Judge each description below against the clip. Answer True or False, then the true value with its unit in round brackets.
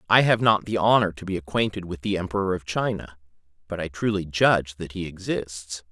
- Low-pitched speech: True (95 Hz)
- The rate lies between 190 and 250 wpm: True (205 wpm)